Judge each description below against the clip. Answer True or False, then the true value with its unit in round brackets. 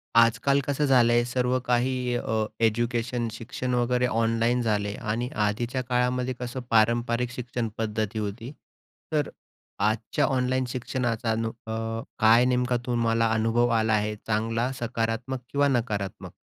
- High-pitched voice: False (120 Hz)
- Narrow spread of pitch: True (1.8 semitones)